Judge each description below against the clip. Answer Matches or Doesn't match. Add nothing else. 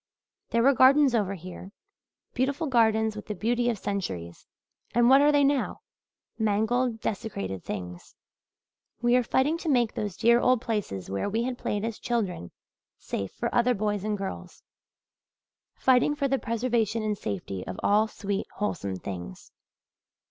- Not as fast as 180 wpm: Matches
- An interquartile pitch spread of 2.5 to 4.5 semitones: Matches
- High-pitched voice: Matches